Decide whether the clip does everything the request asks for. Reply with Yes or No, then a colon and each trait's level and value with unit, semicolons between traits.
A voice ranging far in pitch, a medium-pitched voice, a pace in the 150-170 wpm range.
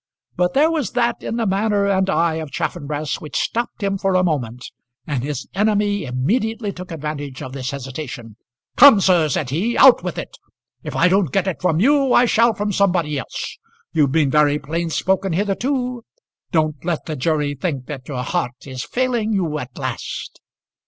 No: wide, 6.1 semitones; medium, 170 Hz; average, 185 wpm